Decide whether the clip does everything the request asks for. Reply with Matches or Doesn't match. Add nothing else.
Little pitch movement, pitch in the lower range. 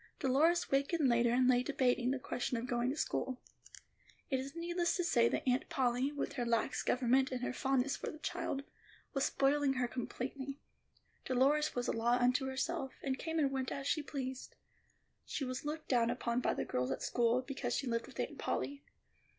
Doesn't match